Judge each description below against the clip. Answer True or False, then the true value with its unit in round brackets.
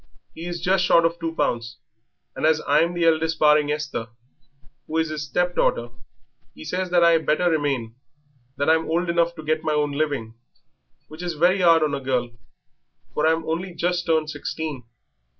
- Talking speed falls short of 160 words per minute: False (185 wpm)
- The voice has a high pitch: False (160 Hz)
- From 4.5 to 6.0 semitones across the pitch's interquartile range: False (2.4 semitones)